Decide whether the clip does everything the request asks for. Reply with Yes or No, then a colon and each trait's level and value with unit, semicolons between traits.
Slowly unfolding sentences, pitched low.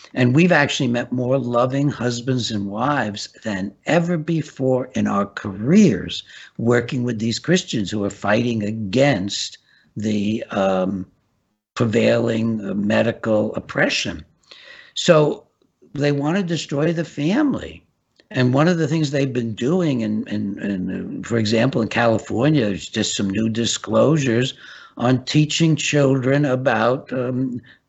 Yes: slow, 130 wpm; low, 120 Hz